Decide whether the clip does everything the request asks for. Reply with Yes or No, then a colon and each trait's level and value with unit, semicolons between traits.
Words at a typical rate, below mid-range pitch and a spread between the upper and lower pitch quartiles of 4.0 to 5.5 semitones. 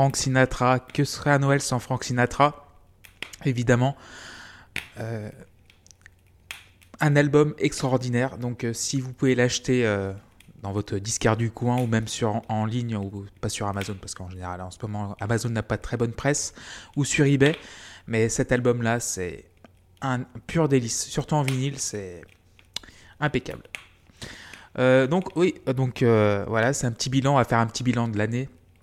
Yes: average, 175 wpm; low, 115 Hz; average, 4.7 semitones